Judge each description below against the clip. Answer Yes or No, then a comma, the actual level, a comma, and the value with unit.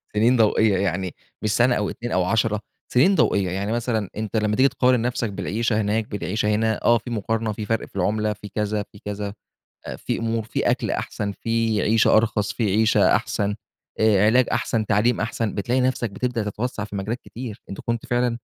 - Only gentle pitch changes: Yes, narrow, 2.1 semitones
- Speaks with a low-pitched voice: Yes, low, 110 Hz